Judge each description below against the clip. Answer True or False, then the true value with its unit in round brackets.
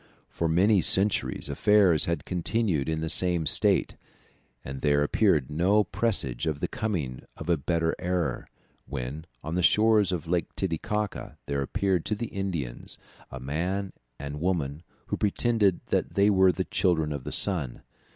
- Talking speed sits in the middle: True (160 wpm)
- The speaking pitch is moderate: False (85 Hz)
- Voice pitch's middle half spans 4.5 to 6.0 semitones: True (4.9 semitones)